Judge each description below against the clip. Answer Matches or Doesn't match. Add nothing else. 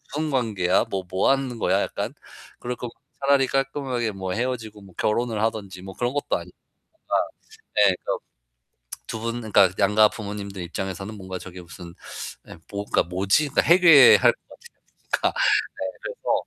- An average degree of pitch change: Matches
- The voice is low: Matches